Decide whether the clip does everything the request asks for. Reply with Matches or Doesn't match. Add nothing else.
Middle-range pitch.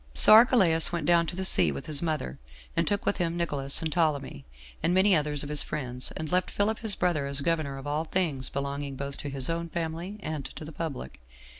Matches